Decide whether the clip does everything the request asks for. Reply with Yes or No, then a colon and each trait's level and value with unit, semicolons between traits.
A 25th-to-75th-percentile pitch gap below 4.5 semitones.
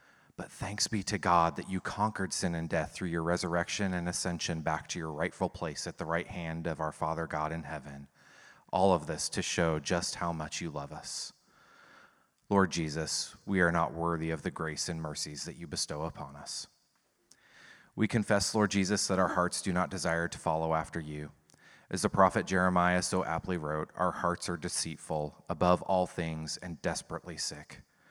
Yes: narrow, 2.4 semitones